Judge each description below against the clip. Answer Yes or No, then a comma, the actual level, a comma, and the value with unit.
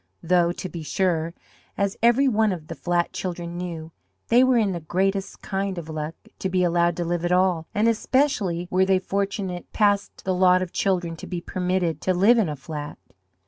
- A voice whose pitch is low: No, medium, 180 Hz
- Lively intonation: No, narrow, 2.4 semitones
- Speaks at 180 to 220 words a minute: Yes, average, 200 wpm